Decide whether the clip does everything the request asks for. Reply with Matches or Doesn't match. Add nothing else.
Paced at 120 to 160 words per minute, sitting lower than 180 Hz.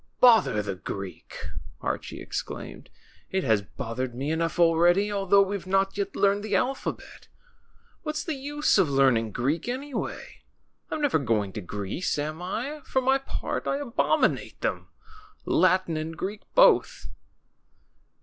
Doesn't match